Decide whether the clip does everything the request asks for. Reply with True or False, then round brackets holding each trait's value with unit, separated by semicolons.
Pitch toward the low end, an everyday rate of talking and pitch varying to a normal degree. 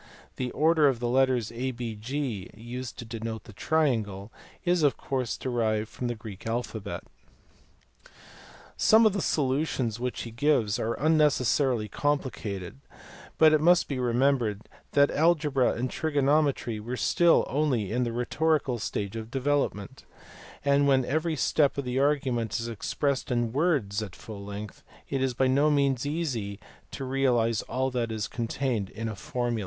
True (125 Hz; 155 wpm; 4.1 semitones)